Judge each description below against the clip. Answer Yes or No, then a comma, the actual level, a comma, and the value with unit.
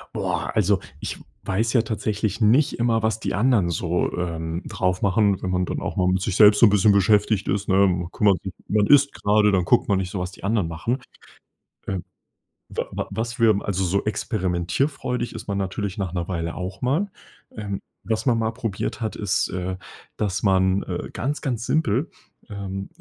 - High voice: No, low, 100 Hz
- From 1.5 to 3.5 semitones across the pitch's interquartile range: Yes, average, 3.2 semitones